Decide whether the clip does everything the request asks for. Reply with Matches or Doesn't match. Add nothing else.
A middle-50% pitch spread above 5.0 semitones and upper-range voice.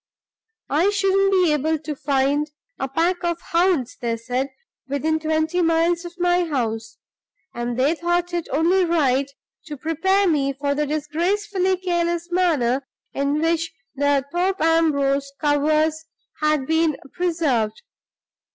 Doesn't match